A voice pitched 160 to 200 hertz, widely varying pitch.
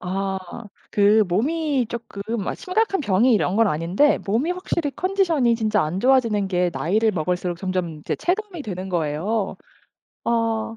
No: high, 215 Hz; wide, 6.3 semitones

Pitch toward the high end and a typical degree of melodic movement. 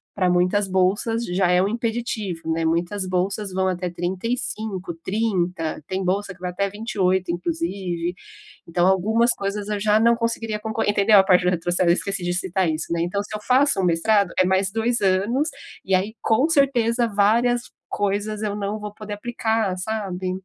Yes: high, 200 Hz; average, 3.3 semitones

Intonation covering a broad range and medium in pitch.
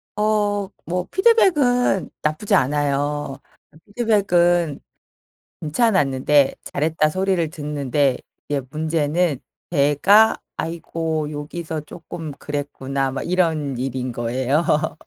No: average, 4.1 semitones; medium, 155 Hz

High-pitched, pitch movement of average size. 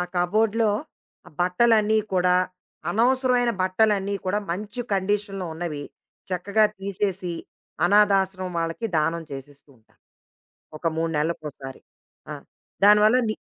Yes: high, 195 Hz; average, 3.6 semitones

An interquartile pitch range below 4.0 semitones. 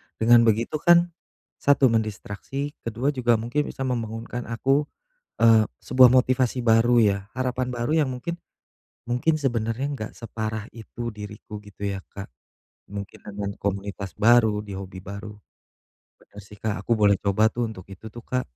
Yes: average, 3.4 semitones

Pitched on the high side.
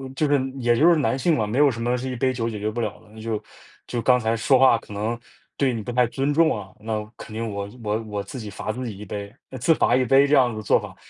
No: low, 115 Hz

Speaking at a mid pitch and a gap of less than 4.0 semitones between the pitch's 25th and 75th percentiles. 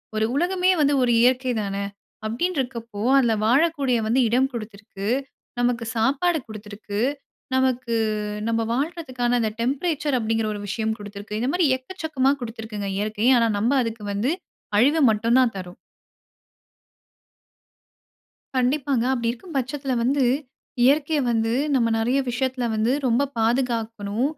No: high, 245 Hz; average, 3.5 semitones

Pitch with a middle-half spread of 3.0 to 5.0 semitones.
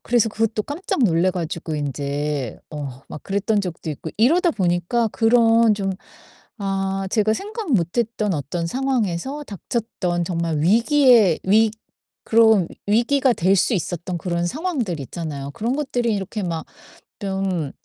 No: wide, 5.5 semitones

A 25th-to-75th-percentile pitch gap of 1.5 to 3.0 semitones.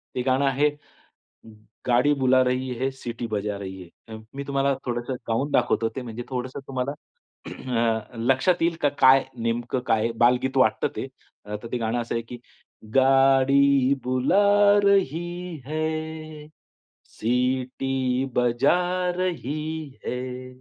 Yes: average, 2.7 semitones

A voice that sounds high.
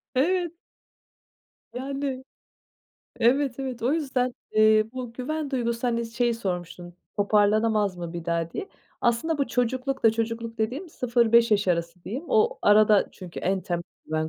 Yes: high, 230 Hz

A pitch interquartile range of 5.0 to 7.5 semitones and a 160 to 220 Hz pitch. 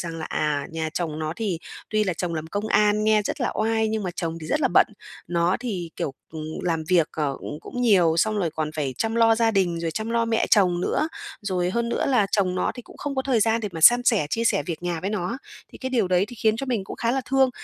Yes: average, 5.3 semitones; high, 200 Hz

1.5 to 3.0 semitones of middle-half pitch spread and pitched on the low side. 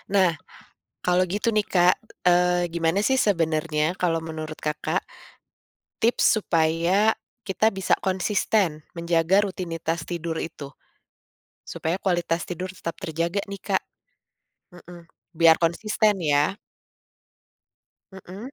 No: average, 2.7 semitones; medium, 175 Hz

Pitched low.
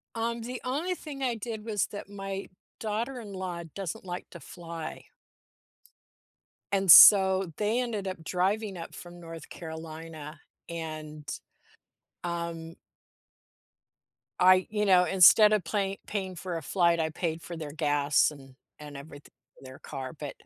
No: medium, 180 Hz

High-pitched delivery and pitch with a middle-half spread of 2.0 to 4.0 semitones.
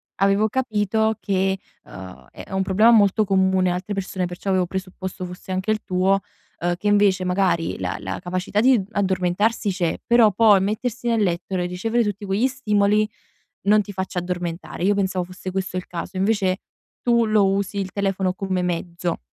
Yes: high, 195 Hz; narrow, 2.4 semitones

